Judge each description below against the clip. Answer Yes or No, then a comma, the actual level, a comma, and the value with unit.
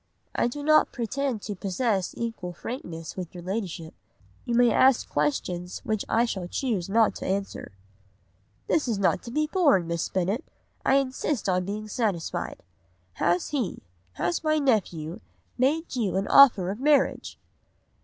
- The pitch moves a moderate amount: No, wide, 6.3 semitones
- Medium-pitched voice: No, high, 215 Hz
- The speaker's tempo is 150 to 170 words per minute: Yes, average, 155 wpm